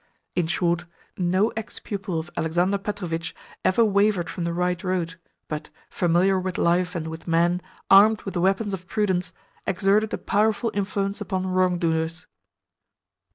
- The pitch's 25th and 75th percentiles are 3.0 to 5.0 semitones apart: No, narrow, 2.5 semitones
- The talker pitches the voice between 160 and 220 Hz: Yes, medium, 185 Hz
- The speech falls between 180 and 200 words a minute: No, average, 150 wpm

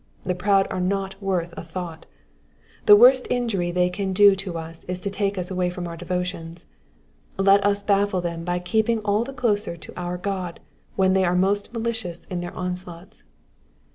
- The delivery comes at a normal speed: Yes, average, 180 wpm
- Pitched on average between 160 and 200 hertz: Yes, medium, 185 Hz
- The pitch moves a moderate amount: No, narrow, 2.3 semitones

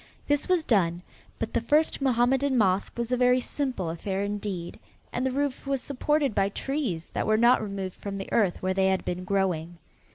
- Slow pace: No, average, 195 wpm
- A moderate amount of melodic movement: No, wide, 5.7 semitones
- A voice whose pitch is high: Yes, high, 215 Hz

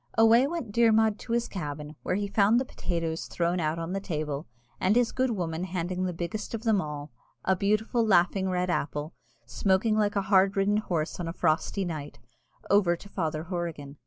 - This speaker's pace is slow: No, average, 190 wpm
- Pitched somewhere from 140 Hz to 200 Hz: Yes, medium, 185 Hz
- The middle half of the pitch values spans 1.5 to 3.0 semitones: No, average, 4.3 semitones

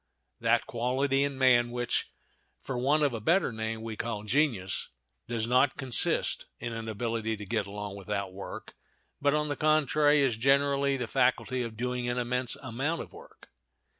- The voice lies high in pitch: No, low, 125 Hz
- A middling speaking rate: Yes, average, 170 wpm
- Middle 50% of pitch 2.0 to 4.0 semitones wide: Yes, average, 3.6 semitones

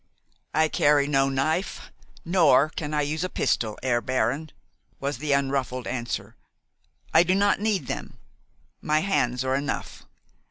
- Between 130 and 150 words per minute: Yes, average, 145 wpm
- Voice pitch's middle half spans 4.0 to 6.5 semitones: No, average, 3.3 semitones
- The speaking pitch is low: No, medium, 145 Hz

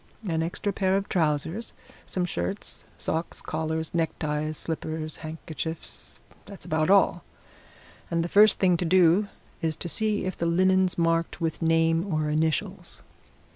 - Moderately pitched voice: Yes, medium, 165 Hz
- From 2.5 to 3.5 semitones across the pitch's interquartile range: Yes, average, 2.8 semitones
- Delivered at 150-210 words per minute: No, average, 140 wpm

